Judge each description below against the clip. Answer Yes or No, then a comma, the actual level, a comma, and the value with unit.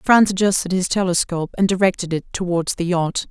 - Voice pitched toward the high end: No, medium, 180 Hz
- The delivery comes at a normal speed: Yes, average, 180 wpm